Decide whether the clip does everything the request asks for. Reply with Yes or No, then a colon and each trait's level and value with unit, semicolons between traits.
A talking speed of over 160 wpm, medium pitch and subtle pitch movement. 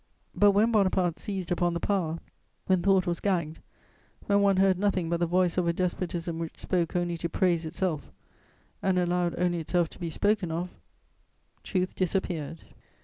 Yes: average, 170 wpm; medium, 180 Hz; narrow, 2.0 semitones